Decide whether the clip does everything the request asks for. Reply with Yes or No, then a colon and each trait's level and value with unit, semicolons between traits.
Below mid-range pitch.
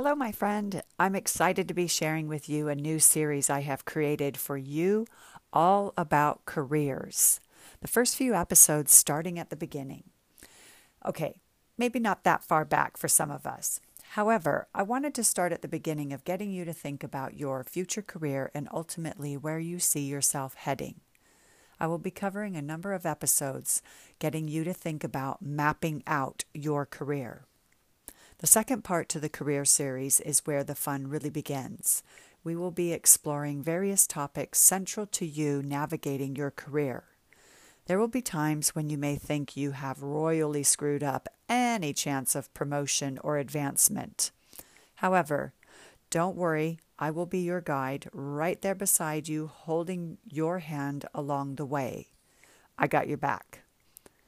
No: medium, 155 Hz